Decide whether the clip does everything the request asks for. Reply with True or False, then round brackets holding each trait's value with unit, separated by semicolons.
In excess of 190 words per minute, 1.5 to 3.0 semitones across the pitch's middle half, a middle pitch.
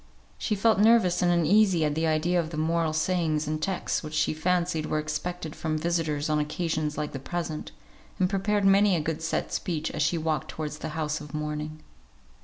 True (200 wpm; 2.6 semitones; 160 Hz)